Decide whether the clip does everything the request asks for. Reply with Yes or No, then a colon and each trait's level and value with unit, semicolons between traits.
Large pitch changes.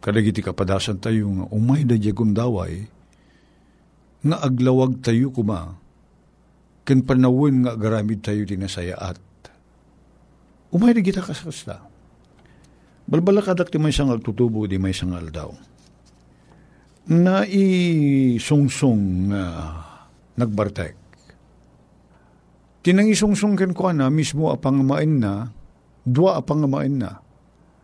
Yes: wide, 7.4 semitones